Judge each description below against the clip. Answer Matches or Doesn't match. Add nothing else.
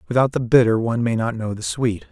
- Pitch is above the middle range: Doesn't match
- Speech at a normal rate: Doesn't match